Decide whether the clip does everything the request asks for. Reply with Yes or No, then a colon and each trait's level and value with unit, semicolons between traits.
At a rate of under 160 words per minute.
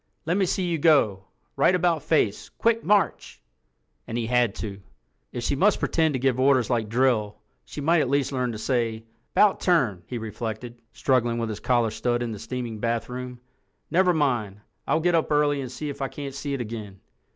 No: average, 195 wpm